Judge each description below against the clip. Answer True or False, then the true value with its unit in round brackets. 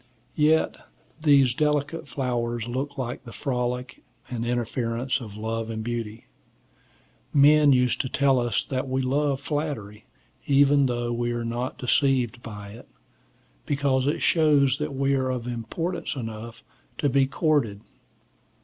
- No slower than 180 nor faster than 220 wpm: False (140 wpm)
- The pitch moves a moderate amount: True (3.1 semitones)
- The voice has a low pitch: True (130 Hz)